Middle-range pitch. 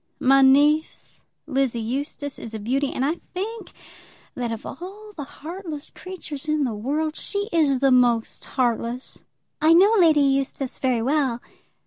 No: very high, 275 Hz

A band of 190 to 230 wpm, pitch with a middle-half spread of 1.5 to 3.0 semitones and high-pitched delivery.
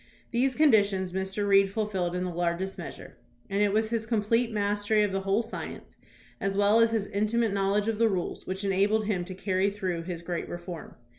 Yes: average, 200 wpm; narrow, 2.5 semitones; high, 200 Hz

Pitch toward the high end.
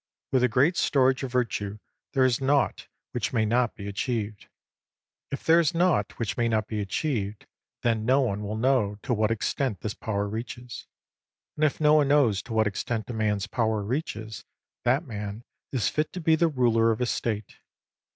No: low, 115 Hz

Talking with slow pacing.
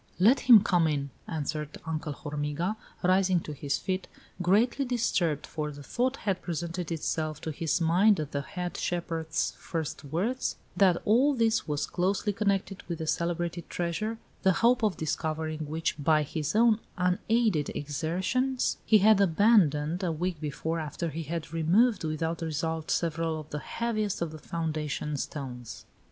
No: average, 155 wpm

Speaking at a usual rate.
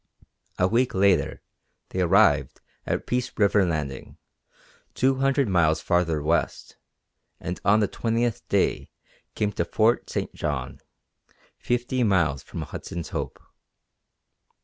No: slow, 120 wpm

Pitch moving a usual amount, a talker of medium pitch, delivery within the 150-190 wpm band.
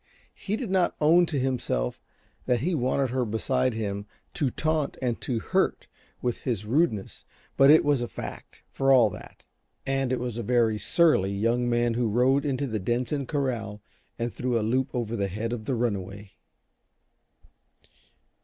No: average, 3.4 semitones; low, 125 Hz; average, 170 wpm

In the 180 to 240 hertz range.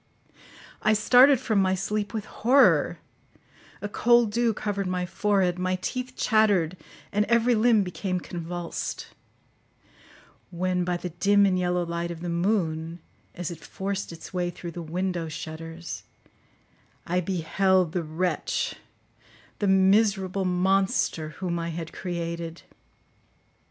Yes: medium, 185 Hz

